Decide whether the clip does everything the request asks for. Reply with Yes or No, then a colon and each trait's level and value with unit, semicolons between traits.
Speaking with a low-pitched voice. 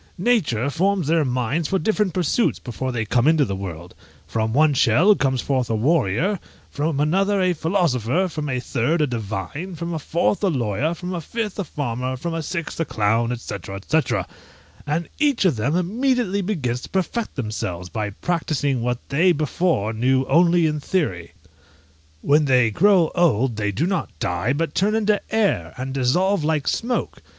No: medium, 150 Hz